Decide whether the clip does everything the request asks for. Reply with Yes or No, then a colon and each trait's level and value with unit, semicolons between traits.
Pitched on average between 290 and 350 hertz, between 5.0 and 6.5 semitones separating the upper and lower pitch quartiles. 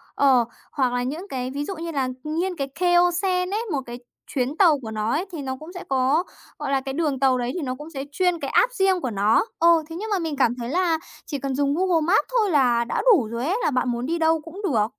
Yes: very high, 295 Hz; wide, 5.5 semitones